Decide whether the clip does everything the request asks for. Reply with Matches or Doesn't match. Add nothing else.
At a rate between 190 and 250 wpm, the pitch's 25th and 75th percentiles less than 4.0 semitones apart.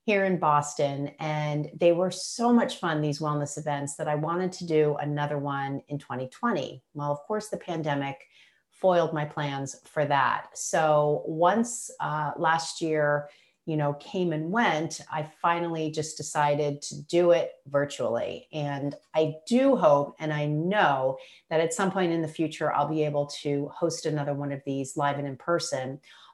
Doesn't match